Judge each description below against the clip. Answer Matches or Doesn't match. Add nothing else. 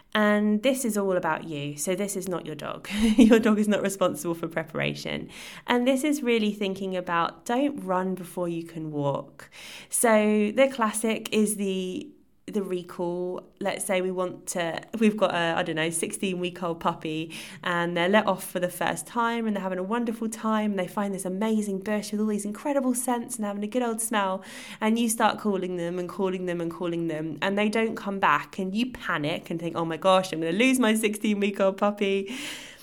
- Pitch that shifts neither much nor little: Matches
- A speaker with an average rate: Doesn't match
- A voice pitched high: Matches